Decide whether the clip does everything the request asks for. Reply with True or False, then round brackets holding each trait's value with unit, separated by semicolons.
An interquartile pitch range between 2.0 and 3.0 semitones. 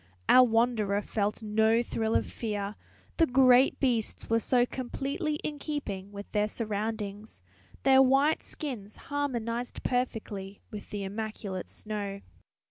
False (3.6 semitones)